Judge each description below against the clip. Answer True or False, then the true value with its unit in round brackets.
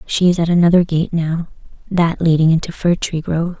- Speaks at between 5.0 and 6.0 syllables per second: True (5.5 syllables/s)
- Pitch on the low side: False (170 Hz)